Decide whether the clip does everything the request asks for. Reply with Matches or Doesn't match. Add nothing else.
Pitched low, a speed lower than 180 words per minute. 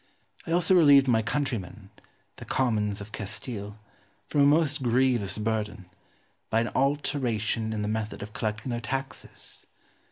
Matches